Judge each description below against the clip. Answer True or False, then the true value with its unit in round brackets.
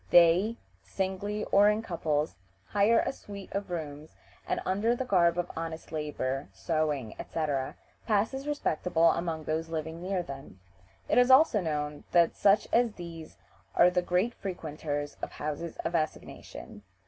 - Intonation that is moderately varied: True (4.5 semitones)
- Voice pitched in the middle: True (170 Hz)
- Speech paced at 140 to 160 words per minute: True (150 wpm)